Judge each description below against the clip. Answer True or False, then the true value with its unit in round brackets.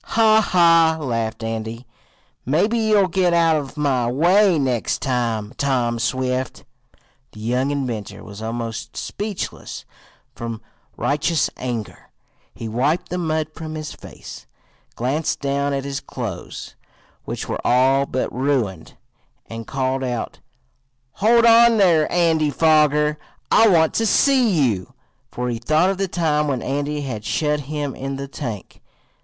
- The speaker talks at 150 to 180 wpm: False (140 wpm)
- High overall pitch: False (140 Hz)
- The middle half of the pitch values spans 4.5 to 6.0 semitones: True (5.1 semitones)